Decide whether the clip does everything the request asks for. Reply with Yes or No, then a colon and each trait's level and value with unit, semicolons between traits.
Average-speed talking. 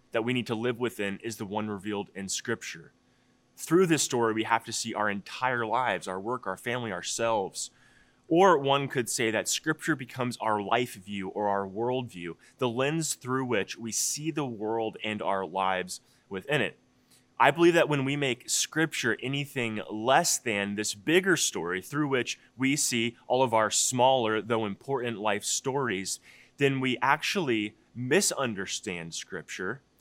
Yes: average, 165 wpm